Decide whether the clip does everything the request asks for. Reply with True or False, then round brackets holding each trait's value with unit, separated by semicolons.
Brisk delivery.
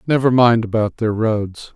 False (170 wpm)